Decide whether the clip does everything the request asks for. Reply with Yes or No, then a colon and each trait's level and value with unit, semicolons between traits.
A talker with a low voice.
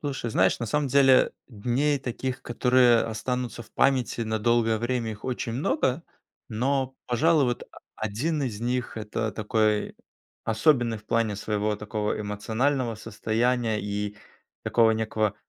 Yes: low, 115 Hz